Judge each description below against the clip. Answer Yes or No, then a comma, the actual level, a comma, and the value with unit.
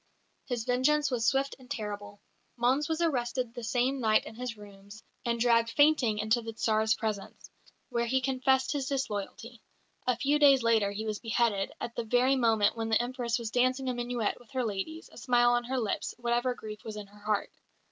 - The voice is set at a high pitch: Yes, high, 240 Hz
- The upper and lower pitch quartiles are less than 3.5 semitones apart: Yes, average, 2.9 semitones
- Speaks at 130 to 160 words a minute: No, average, 200 wpm